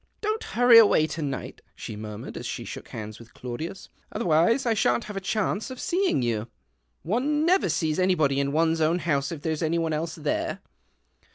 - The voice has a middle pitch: Yes, medium, 165 Hz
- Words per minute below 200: No, fast, 205 wpm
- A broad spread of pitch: Yes, wide, 7.3 semitones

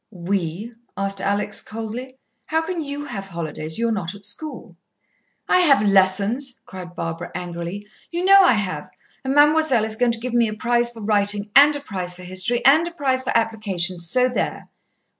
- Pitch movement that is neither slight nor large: No, wide, 5.7 semitones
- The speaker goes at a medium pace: Yes, average, 180 wpm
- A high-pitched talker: Yes, high, 220 Hz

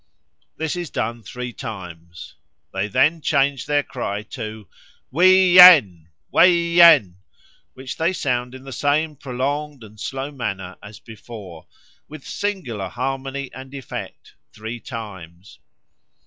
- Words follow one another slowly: Yes, slow, 125 wpm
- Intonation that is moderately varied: No, wide, 5.7 semitones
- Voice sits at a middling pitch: No, low, 130 Hz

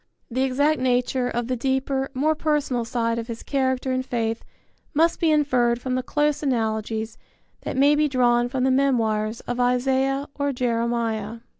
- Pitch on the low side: No, very high, 255 Hz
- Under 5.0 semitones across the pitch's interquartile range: Yes, narrow, 2.6 semitones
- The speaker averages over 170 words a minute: No, average, 165 wpm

